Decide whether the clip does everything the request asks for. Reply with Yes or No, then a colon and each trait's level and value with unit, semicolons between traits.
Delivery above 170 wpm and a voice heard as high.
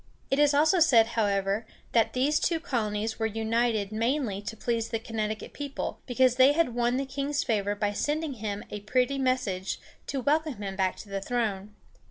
Yes: average, 185 wpm; high, 230 Hz